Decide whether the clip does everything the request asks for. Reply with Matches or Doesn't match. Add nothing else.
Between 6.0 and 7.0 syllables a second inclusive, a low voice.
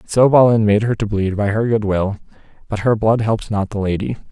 Matches